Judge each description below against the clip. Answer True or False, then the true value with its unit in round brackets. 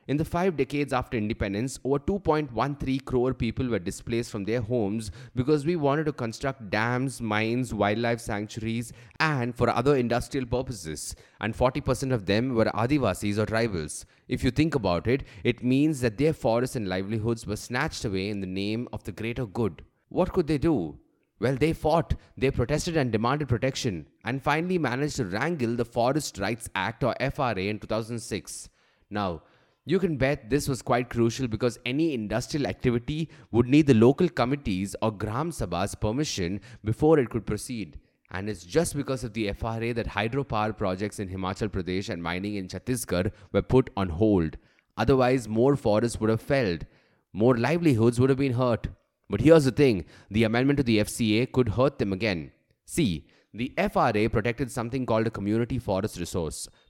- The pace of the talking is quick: False (175 wpm)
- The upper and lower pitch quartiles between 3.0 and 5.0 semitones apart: True (4.3 semitones)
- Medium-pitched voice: False (120 Hz)